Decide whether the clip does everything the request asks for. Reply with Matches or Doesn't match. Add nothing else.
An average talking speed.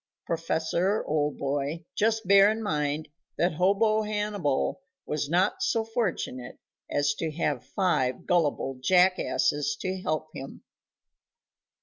Doesn't match